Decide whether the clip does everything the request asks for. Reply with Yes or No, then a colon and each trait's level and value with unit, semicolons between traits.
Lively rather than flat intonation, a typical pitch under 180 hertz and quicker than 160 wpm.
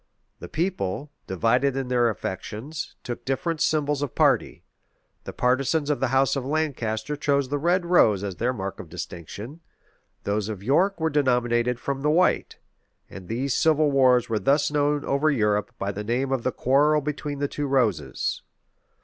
No: average, 4.5 semitones; low, 135 Hz; average, 170 wpm